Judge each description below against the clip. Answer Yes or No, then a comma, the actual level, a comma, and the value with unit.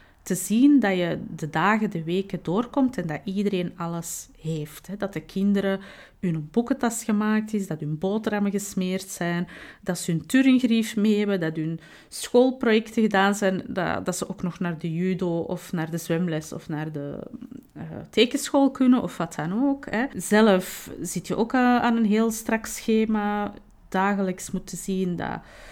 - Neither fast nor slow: Yes, average, 165 wpm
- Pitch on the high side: Yes, high, 195 Hz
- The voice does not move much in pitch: No, average, 4.2 semitones